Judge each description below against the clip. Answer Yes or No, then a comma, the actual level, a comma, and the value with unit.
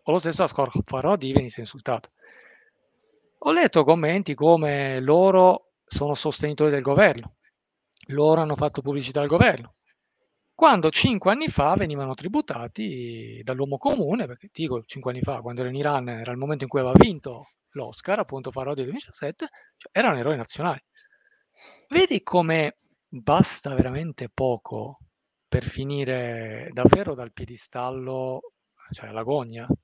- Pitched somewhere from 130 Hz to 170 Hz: Yes, medium, 140 Hz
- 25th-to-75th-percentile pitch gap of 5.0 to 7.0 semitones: Yes, wide, 5.5 semitones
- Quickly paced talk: No, average, 135 wpm